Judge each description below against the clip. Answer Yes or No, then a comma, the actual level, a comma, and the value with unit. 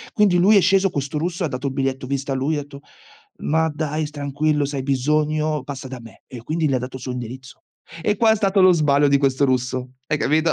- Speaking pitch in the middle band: Yes, medium, 145 Hz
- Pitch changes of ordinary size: Yes, average, 3.0 semitones